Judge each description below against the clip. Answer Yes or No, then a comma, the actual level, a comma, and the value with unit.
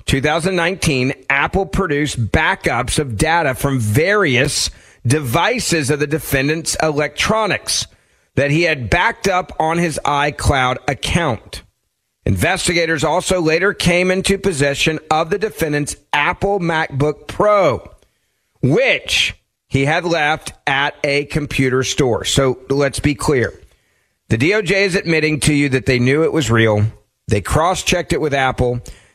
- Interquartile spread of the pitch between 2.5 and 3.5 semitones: No, average, 4.4 semitones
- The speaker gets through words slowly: Yes, slow, 130 wpm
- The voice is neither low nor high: Yes, medium, 150 Hz